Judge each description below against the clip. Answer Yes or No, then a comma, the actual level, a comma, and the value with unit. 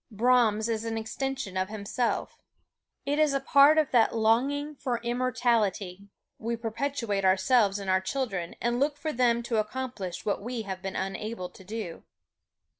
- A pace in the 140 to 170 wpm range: Yes, average, 160 wpm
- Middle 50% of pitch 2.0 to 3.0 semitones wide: No, average, 4.1 semitones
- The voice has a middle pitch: No, high, 230 Hz